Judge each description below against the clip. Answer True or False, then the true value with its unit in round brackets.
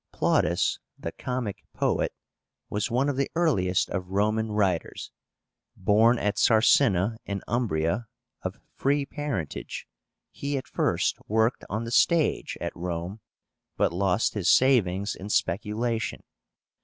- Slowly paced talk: True (125 wpm)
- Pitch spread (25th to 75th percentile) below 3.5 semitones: False (4.4 semitones)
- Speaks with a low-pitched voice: True (110 Hz)